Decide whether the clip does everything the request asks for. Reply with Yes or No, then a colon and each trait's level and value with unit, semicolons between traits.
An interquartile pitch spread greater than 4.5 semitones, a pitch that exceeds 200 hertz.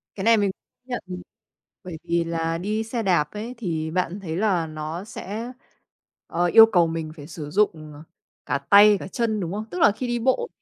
No: average, 4.9 semitones; medium, 185 Hz